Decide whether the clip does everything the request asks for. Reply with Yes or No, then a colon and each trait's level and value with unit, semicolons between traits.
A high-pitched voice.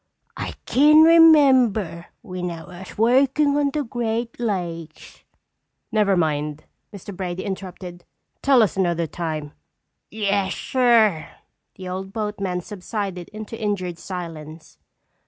Yes: high, 195 Hz